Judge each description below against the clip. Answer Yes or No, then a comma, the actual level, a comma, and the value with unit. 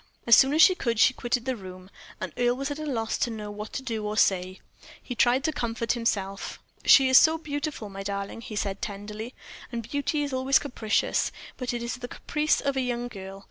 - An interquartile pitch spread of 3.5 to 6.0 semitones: Yes, average, 4.2 semitones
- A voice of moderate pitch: No, high, 235 Hz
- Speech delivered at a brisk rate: Yes, fast, 220 wpm